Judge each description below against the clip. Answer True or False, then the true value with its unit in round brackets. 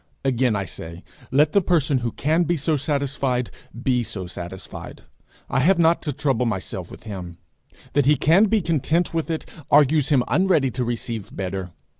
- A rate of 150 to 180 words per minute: True (175 wpm)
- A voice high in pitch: False (135 Hz)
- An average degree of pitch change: False (5.7 semitones)